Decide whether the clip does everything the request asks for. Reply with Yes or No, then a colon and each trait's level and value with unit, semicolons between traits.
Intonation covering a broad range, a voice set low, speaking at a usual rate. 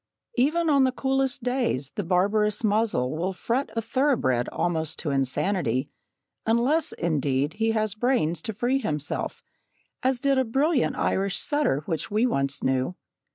No: wide, 8.8 semitones; high, 215 Hz; average, 150 wpm